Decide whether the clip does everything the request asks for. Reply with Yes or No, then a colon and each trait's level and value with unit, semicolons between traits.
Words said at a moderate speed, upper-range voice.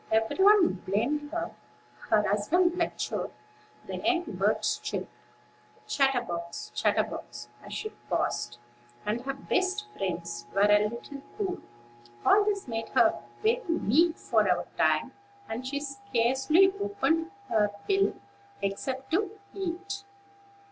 No: slow, 120 wpm; very high, 280 Hz